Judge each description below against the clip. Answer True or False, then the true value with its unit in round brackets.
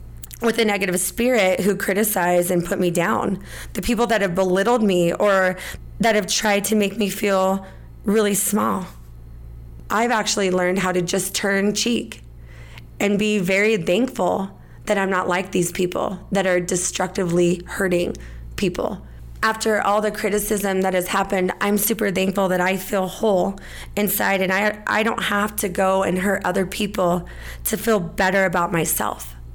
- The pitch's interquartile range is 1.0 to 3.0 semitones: True (2.5 semitones)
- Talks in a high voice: True (195 Hz)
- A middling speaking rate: True (160 wpm)